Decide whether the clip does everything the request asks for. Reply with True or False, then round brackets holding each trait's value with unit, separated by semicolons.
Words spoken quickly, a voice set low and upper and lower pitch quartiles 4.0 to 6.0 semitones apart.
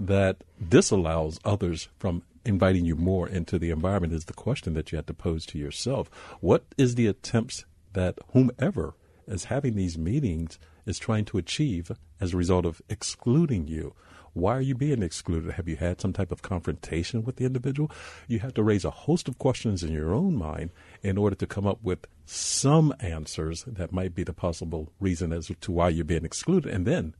False (195 wpm; 90 Hz; 5.1 semitones)